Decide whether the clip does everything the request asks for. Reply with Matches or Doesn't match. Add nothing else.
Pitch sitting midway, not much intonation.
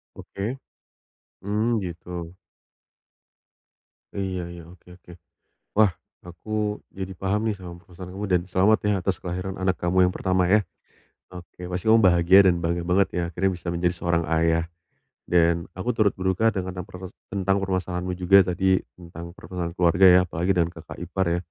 Doesn't match